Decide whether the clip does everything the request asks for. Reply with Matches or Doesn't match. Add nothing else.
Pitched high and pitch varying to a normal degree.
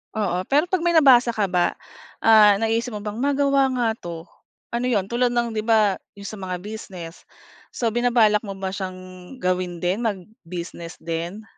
Matches